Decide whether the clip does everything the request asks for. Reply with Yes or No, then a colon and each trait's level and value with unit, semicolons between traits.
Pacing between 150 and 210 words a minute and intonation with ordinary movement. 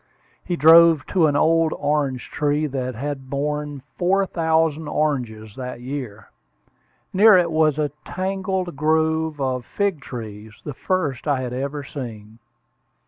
No: average, 140 wpm; average, 3.9 semitones